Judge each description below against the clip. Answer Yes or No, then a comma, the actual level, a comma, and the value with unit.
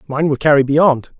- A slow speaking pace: No, average, 200 wpm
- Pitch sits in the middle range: Yes, medium, 145 Hz